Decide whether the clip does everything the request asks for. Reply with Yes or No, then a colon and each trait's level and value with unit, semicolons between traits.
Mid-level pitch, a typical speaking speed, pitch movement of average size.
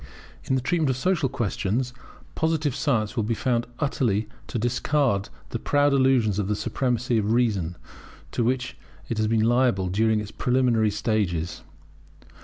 No: low, 120 Hz; average, 155 wpm; average, 3.6 semitones